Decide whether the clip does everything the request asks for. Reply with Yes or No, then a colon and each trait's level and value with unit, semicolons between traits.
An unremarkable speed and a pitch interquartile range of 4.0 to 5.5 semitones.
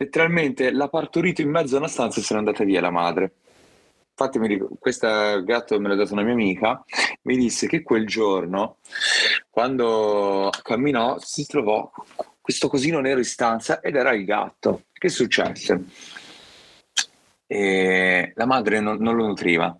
Yes: average, 150 wpm; average, 4.7 semitones